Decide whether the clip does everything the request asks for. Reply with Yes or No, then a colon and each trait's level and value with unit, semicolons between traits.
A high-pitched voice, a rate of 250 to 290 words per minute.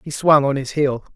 No: medium, 140 Hz; fast, 260 wpm